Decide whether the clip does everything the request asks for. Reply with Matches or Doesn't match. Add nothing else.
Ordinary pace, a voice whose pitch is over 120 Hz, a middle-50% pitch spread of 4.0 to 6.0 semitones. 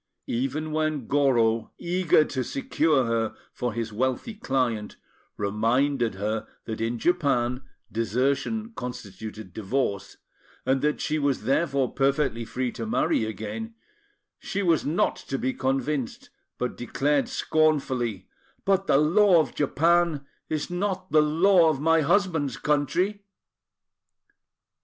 Doesn't match